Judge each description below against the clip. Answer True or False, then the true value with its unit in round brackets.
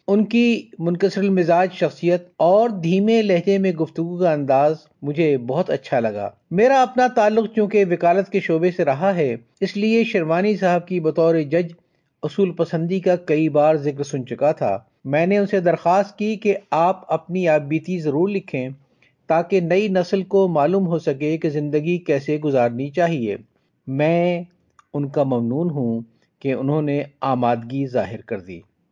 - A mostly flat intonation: False (4.6 semitones)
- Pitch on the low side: False (170 Hz)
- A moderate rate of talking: True (160 wpm)